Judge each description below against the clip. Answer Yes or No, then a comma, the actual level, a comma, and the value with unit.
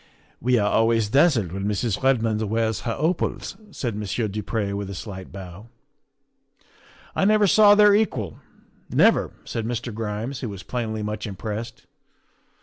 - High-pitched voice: No, low, 110 Hz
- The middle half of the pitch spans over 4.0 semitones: No, average, 3.3 semitones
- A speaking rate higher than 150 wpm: Yes, average, 160 wpm